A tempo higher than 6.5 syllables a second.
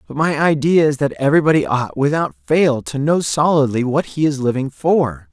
No: 5.1 syllables/s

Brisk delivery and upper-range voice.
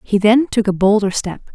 Yes: fast, 235 wpm; high, 210 Hz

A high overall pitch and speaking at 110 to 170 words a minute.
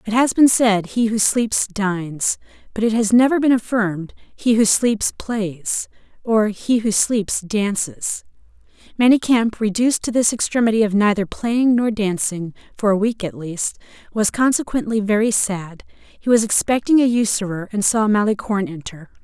Yes: high, 215 Hz; average, 150 wpm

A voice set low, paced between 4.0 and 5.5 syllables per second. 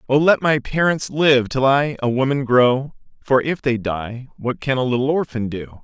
Yes: low, 130 Hz; 4.6 syllables/s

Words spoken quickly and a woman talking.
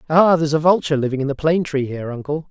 No: fast, 265 wpm; male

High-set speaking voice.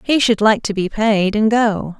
Yes: high, 215 Hz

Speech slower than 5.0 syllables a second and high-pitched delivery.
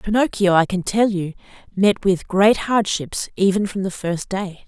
Yes: 4.3 syllables/s; high, 195 Hz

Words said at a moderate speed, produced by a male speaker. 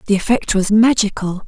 No: average, 165 wpm; female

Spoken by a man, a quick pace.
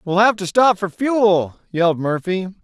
No: male; average, 180 wpm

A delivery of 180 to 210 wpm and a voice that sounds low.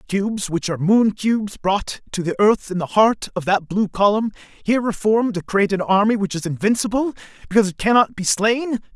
No: average, 200 wpm; high, 205 Hz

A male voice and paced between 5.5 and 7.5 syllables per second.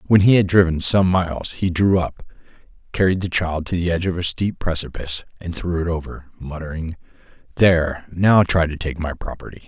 Yes: male; 5.6 syllables/s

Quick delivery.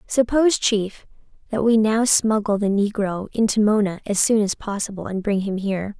No: average, 180 wpm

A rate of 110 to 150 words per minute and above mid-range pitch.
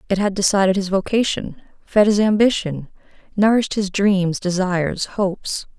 Yes: slow, 135 wpm; high, 195 Hz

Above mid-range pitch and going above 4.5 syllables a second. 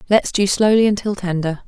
Yes: high, 200 Hz; 5.5 syllables/s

